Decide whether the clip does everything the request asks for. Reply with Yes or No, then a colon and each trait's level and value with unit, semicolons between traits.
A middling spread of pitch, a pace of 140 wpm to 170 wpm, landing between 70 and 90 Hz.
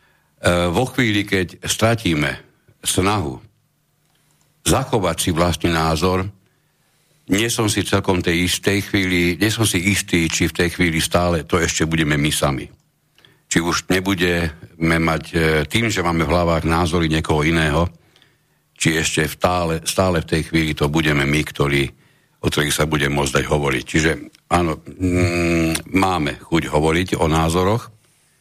Yes: average, 3.4 semitones; average, 150 wpm; very low, 85 Hz